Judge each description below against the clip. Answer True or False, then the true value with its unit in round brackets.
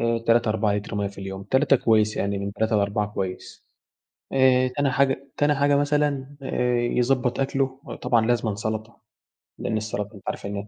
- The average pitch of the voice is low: True (115 Hz)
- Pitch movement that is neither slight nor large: True (4.5 semitones)